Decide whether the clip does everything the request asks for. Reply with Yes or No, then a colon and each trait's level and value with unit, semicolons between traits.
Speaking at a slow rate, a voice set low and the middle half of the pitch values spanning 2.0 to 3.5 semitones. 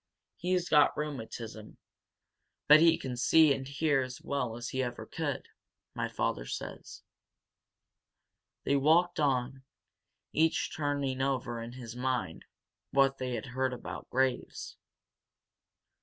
Yes: slow, 125 wpm; low, 130 Hz; average, 3.0 semitones